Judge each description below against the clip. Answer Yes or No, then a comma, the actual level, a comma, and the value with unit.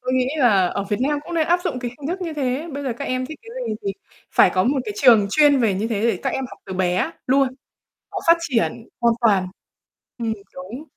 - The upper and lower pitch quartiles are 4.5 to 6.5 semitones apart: Yes, average, 4.9 semitones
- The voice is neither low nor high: No, very high, 255 Hz